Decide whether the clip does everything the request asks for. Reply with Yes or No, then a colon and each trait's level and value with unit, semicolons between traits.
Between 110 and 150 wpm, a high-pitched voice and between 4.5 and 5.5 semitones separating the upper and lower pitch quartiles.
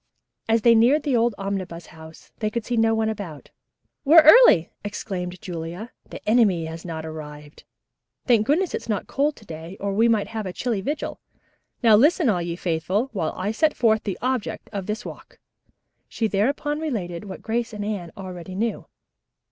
No: average, 180 wpm; high, 210 Hz; average, 4.9 semitones